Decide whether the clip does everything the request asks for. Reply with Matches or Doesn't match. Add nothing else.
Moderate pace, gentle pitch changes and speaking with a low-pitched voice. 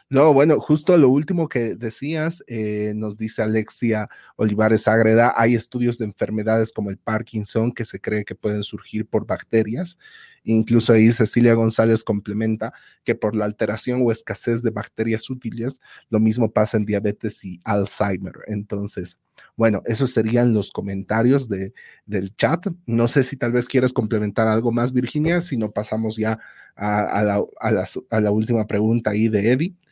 Matches